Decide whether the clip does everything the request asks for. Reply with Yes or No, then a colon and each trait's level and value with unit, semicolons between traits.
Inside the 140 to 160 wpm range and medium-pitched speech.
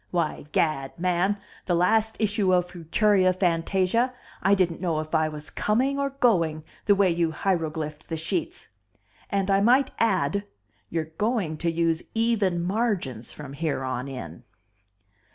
Yes: average, 150 wpm; medium, 180 Hz